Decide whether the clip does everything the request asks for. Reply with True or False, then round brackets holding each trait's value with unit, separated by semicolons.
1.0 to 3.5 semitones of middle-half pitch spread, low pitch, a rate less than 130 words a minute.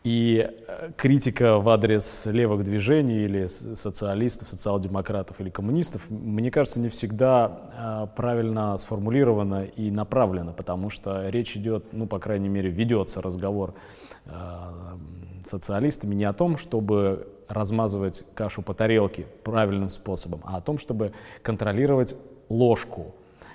True (3.0 semitones; 105 Hz; 120 wpm)